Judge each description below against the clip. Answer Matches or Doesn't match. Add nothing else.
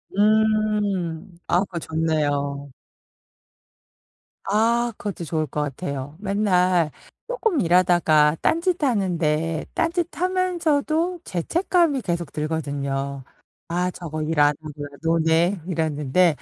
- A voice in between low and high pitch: Matches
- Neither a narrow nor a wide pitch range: Doesn't match